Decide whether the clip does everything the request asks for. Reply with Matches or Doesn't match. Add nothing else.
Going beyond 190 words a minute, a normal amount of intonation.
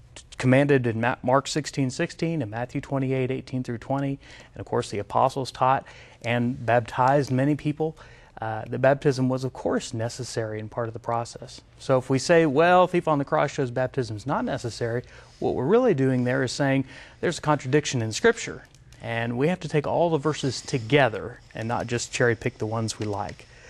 Matches